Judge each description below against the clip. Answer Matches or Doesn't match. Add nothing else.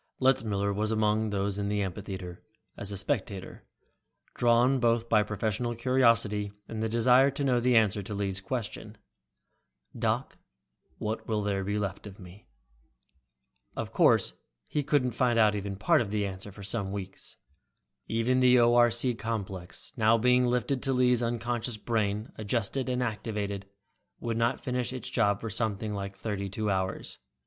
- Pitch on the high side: Doesn't match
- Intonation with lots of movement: Doesn't match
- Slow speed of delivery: Doesn't match